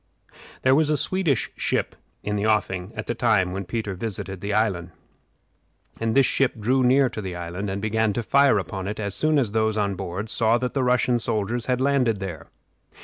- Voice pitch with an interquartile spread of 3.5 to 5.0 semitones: Yes, average, 4.2 semitones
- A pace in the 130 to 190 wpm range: No, fast, 205 wpm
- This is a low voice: Yes, low, 110 Hz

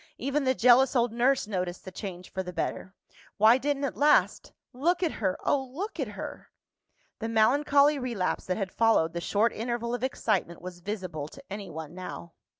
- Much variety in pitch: Yes, wide, 6.4 semitones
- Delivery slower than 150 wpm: No, average, 180 wpm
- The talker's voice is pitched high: Yes, high, 225 Hz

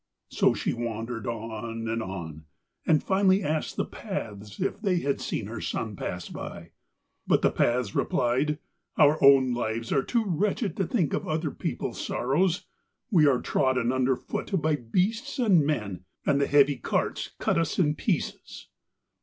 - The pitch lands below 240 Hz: Yes, low, 135 Hz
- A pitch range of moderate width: No, wide, 6.4 semitones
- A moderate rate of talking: Yes, average, 165 wpm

